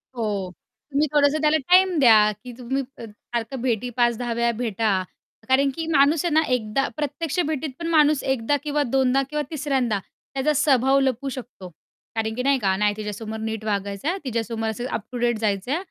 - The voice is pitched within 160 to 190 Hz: No, very high, 250 Hz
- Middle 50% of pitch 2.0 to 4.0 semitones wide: No, average, 4.5 semitones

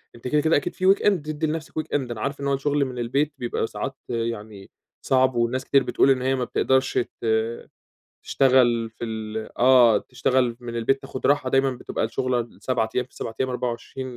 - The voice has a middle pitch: No, low, 130 Hz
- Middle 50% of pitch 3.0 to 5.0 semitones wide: No, narrow, 2.6 semitones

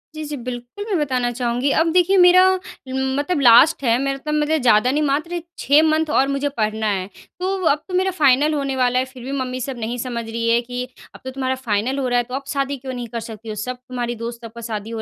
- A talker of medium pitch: No, very high, 260 Hz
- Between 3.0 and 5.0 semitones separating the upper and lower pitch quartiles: Yes, average, 3.6 semitones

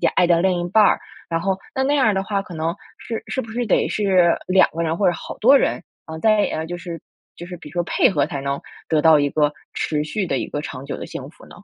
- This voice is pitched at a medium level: Yes, medium, 175 Hz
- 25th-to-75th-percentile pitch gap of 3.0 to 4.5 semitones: Yes, average, 4.0 semitones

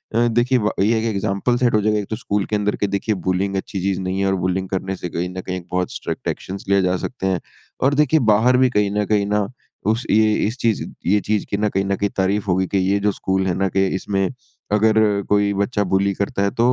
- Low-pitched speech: Yes, low, 100 Hz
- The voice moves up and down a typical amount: No, narrow, 2.0 semitones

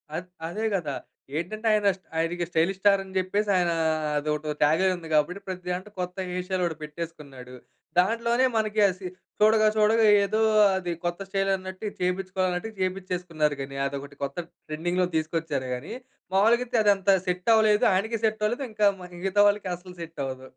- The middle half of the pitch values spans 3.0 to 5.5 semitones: Yes, average, 3.9 semitones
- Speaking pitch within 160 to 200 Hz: Yes, medium, 185 Hz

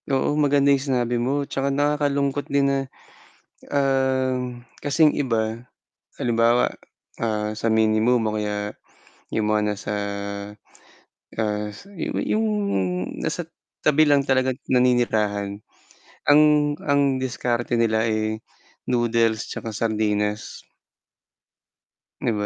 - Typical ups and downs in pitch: Yes, average, 4.1 semitones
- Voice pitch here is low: Yes, low, 120 Hz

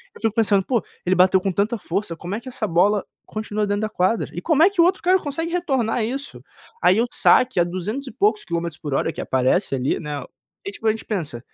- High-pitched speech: Yes, high, 210 Hz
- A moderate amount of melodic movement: No, wide, 5.8 semitones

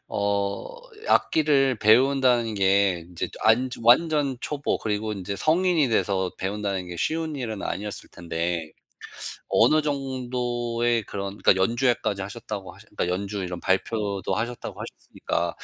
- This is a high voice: No, low, 110 Hz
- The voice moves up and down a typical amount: Yes, average, 4.9 semitones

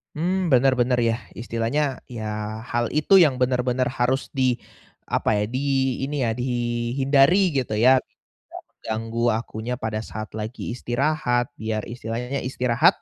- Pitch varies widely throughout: No, average, 2.8 semitones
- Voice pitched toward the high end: No, low, 125 Hz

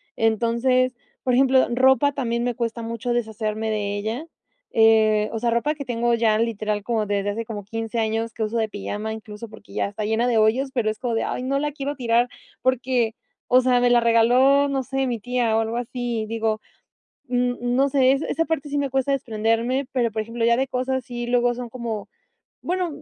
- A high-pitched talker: Yes, high, 235 Hz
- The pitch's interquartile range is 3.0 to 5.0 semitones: No, narrow, 2.6 semitones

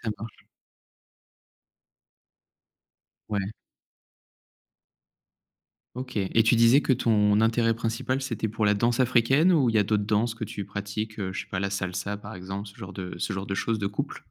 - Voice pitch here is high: No, low, 110 Hz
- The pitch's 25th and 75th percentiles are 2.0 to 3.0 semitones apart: Yes, narrow, 2.6 semitones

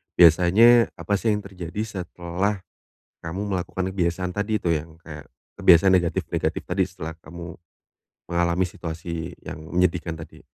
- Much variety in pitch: No, narrow, 2.4 semitones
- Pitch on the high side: No, very low, 90 Hz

